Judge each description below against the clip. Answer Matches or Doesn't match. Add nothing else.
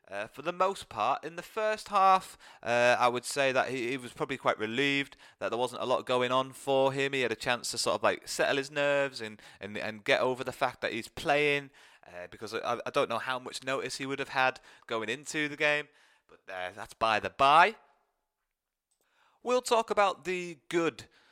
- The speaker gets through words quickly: Matches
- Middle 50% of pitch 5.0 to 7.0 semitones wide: Matches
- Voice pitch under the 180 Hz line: Matches